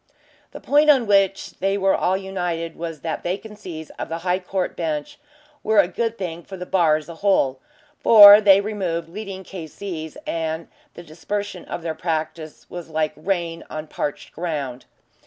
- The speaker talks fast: No, average, 170 wpm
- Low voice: No, medium, 175 Hz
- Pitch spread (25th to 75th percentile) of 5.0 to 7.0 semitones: No, average, 3.5 semitones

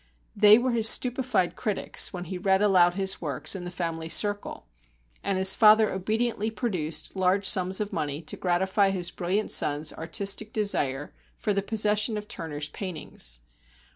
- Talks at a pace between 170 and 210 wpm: No, average, 160 wpm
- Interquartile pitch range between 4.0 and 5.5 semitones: No, average, 3.3 semitones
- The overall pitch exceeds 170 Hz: Yes, high, 190 Hz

